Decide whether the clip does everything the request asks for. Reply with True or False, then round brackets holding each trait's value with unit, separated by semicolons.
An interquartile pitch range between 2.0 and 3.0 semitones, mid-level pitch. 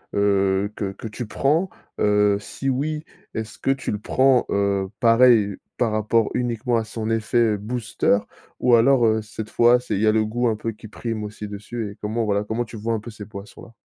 False (2.5 semitones; 110 Hz)